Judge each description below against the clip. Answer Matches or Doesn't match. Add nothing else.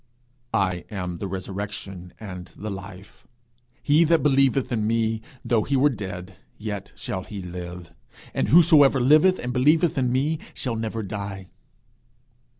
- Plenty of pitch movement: Matches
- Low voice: Matches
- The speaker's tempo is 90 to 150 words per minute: Matches